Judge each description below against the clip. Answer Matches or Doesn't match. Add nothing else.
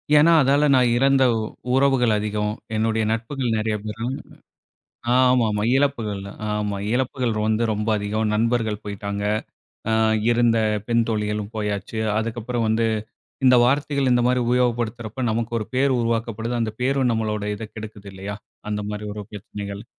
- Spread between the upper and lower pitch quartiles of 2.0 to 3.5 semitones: Matches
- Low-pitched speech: Matches